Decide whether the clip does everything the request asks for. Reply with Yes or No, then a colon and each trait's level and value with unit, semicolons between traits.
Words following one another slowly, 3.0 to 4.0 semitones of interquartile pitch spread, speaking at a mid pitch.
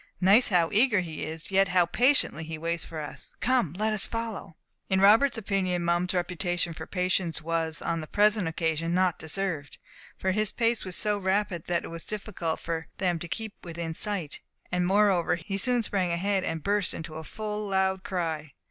No: average, 190 wpm; average, 3.6 semitones; medium, 180 Hz